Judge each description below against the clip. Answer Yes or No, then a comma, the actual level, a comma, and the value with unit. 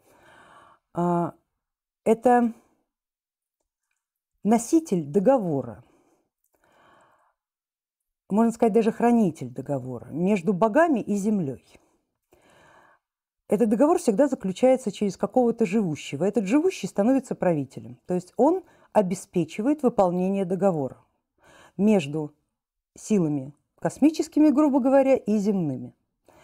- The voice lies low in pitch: No, high, 205 Hz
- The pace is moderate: No, slow, 85 wpm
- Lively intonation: Yes, wide, 7.2 semitones